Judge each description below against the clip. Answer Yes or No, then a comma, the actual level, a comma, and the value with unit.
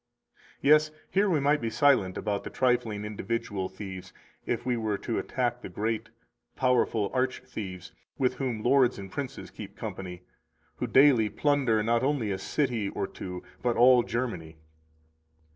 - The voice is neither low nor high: No, low, 115 Hz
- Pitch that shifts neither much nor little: Yes, average, 4.1 semitones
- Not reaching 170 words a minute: Yes, average, 160 wpm